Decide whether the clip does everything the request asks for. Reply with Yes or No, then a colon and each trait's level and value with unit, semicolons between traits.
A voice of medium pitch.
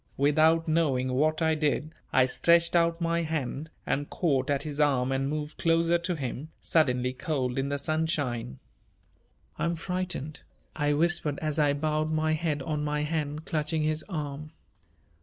Yes: medium, 155 Hz